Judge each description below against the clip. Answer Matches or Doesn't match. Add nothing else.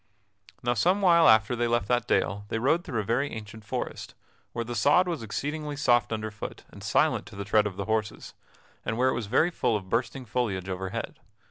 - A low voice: Matches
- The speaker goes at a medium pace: Doesn't match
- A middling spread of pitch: Matches